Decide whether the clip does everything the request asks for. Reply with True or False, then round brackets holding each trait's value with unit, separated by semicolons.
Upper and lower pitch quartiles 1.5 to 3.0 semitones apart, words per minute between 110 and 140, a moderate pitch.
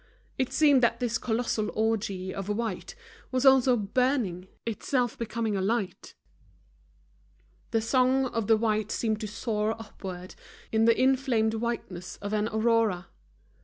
False (2.6 semitones; 135 wpm; 225 Hz)